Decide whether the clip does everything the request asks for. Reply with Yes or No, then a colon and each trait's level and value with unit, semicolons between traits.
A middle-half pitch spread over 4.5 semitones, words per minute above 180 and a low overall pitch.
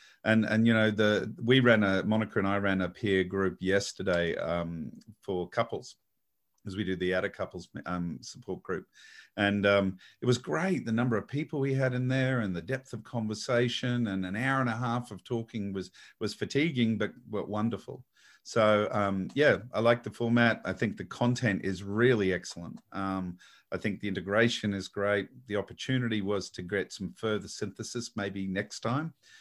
No: average, 3.3 semitones; average, 190 wpm; low, 105 Hz